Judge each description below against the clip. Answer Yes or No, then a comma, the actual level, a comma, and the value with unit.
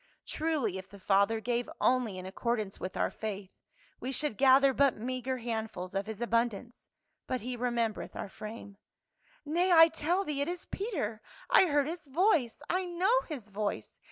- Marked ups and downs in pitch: Yes, wide, 6.0 semitones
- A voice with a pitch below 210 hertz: No, high, 245 Hz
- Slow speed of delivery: No, average, 180 wpm